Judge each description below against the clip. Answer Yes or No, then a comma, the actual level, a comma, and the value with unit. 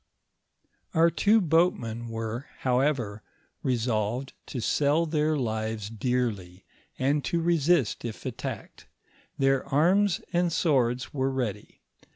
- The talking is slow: Yes, slow, 110 wpm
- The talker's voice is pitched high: No, low, 130 Hz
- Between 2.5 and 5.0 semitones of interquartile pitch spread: No, wide, 5.6 semitones